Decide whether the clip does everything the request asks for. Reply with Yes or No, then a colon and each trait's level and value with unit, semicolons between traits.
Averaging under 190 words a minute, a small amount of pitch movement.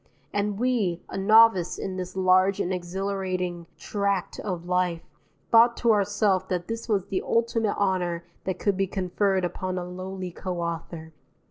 Yes: average, 155 wpm; narrow, 2.1 semitones